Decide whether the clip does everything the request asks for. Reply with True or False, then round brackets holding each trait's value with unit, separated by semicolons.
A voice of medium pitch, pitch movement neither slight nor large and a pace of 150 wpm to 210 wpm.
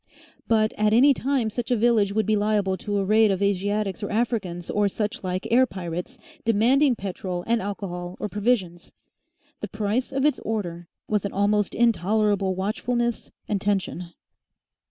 False (210 Hz; 3.1 semitones; 160 wpm)